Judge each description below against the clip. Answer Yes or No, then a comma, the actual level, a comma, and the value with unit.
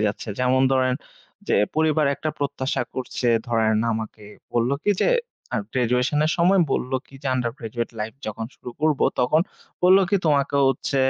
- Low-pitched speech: Yes, low, 130 Hz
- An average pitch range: Yes, average, 3.9 semitones